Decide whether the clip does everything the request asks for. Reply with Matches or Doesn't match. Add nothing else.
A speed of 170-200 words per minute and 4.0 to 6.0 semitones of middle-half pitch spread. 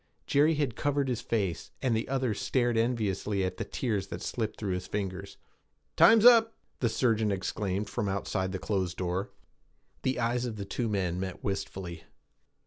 Matches